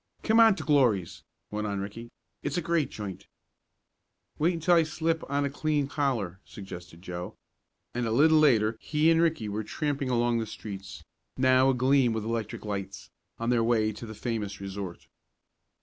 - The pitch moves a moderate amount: No, wide, 6.3 semitones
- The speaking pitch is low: Yes, low, 120 Hz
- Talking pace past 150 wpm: Yes, average, 170 wpm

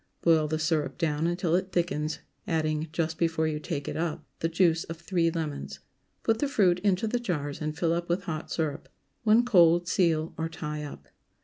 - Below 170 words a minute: No, average, 195 wpm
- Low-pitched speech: No, medium, 165 Hz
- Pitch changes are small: Yes, narrow, 2.1 semitones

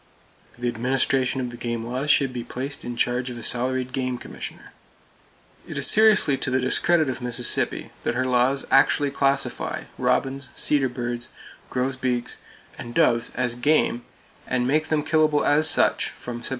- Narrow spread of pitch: Yes, narrow, 2.2 semitones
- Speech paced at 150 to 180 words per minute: Yes, average, 165 wpm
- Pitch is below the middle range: Yes, low, 130 Hz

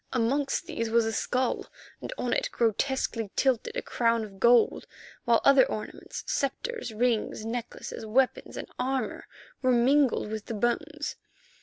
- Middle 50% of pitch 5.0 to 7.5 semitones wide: No, average, 2.9 semitones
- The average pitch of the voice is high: Yes, high, 240 Hz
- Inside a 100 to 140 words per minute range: Yes, slow, 135 wpm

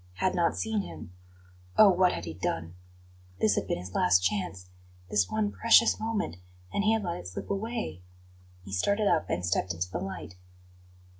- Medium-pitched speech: Yes, medium, 170 Hz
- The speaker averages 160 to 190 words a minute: Yes, average, 180 wpm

